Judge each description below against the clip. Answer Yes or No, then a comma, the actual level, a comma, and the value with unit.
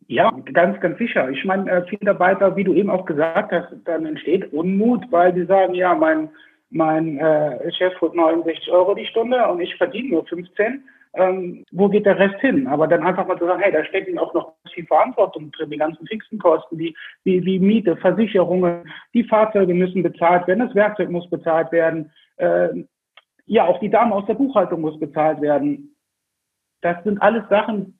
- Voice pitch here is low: No, medium, 180 Hz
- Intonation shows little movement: No, average, 3.6 semitones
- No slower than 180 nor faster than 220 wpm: Yes, fast, 190 wpm